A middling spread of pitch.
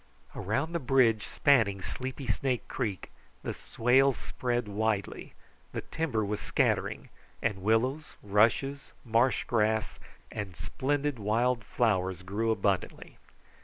Yes: average, 4.0 semitones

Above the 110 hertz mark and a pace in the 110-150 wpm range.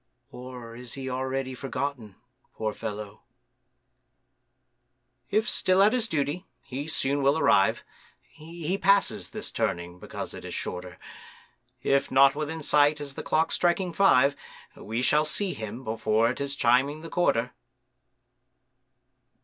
Yes: medium, 140 Hz; slow, 135 wpm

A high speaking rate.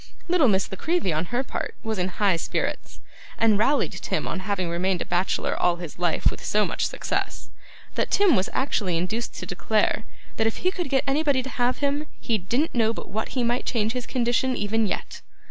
Yes: fast, 210 wpm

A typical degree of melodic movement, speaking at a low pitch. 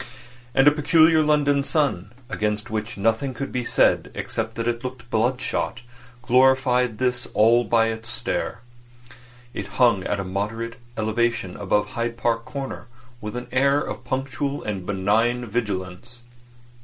Yes: average, 3.2 semitones; low, 120 Hz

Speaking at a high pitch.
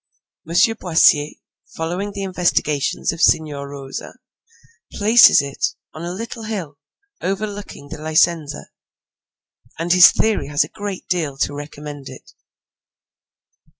No: medium, 165 Hz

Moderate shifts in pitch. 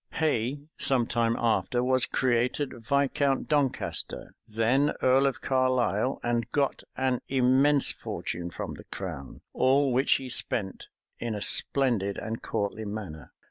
Yes: average, 3.2 semitones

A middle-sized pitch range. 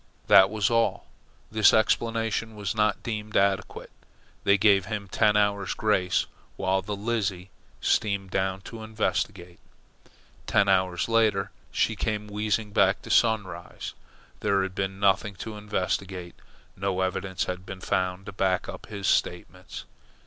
No: narrow, 2.2 semitones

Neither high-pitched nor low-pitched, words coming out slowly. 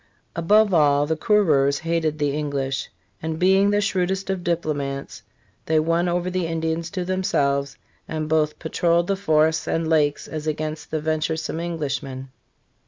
No: medium, 160 Hz; average, 155 wpm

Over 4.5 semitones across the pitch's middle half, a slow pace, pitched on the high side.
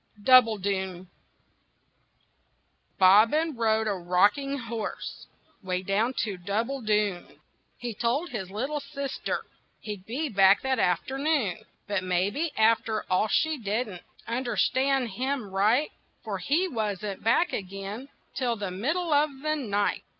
Yes: average, 5.2 semitones; slow, 120 wpm; high, 220 Hz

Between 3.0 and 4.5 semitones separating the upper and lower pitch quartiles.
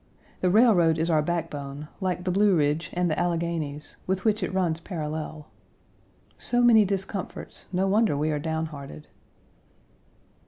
Yes: average, 3.6 semitones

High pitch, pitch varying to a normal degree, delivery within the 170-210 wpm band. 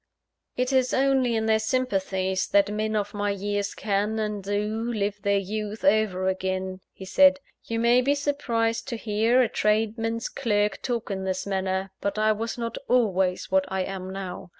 Yes: high, 210 Hz; average, 3.0 semitones; average, 175 wpm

